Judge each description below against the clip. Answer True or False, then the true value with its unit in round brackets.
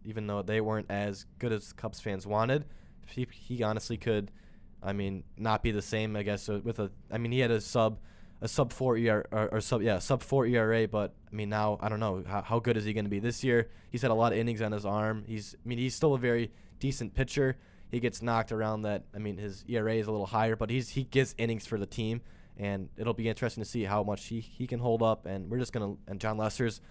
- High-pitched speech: False (110 Hz)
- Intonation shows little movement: True (2.3 semitones)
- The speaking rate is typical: False (265 wpm)